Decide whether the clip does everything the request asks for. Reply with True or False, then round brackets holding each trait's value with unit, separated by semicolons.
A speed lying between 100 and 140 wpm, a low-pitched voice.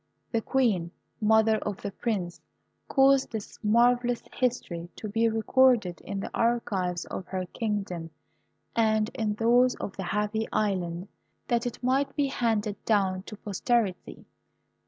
False (135 wpm; 220 Hz)